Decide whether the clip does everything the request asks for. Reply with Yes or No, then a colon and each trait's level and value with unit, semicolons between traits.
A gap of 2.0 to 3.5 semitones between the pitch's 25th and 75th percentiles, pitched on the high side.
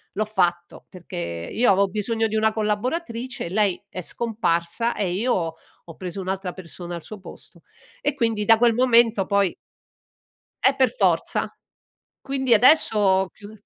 No: average, 4.0 semitones; high, 210 Hz